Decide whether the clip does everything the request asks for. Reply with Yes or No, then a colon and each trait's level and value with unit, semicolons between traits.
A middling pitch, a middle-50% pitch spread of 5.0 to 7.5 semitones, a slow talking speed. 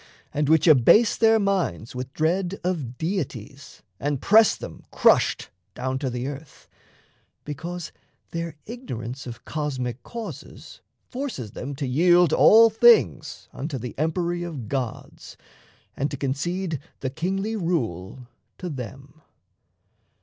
Yes: medium, 150 Hz; wide, 5.6 semitones; slow, 125 wpm